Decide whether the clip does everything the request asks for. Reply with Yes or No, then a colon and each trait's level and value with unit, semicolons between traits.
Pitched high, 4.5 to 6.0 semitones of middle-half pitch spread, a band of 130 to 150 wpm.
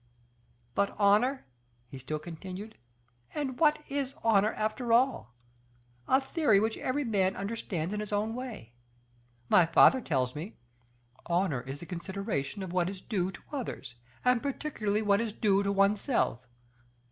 Yes: high, 205 Hz; average, 5.1 semitones; average, 145 wpm